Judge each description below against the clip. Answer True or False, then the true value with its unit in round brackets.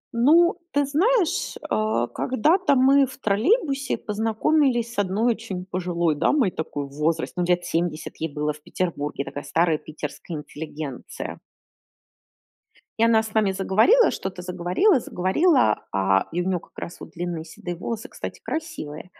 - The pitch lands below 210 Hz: True (190 Hz)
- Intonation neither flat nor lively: False (8.6 semitones)